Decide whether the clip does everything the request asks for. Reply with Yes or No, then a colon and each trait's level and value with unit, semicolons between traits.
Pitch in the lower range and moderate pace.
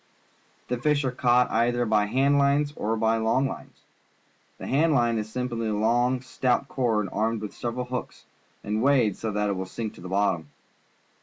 Yes: low, 120 Hz; average, 185 wpm